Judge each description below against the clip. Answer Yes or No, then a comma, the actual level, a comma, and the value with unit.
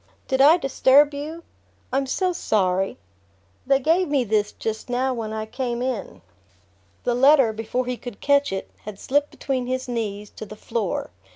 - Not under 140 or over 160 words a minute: No, average, 170 wpm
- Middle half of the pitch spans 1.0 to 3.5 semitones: No, average, 4.2 semitones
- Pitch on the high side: Yes, very high, 250 Hz